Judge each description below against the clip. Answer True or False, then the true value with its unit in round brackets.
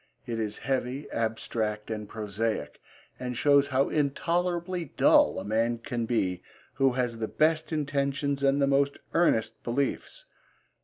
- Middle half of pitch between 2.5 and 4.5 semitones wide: True (4.1 semitones)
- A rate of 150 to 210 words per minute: False (140 wpm)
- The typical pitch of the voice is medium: False (130 Hz)